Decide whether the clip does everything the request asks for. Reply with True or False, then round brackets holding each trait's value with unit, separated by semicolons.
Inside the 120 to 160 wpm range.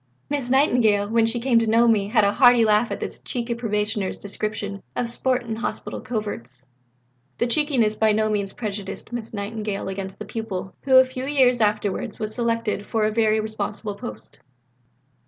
False (175 wpm)